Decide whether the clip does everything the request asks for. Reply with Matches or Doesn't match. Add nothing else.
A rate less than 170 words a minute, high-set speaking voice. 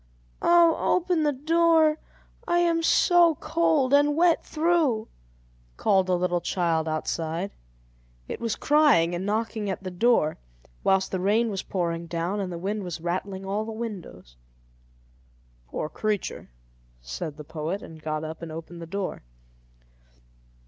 Matches